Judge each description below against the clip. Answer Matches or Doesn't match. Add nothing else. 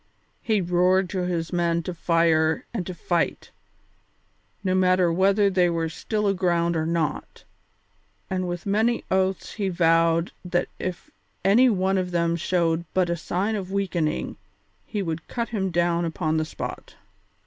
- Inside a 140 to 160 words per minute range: Matches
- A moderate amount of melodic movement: Doesn't match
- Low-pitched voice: Doesn't match